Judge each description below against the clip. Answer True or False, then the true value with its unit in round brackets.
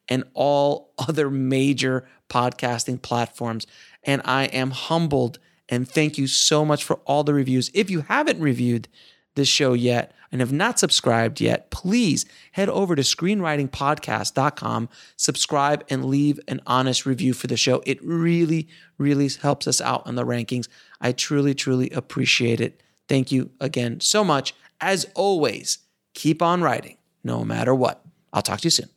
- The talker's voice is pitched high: False (135 Hz)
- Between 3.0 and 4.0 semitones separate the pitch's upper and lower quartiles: True (3.3 semitones)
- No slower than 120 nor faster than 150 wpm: False (160 wpm)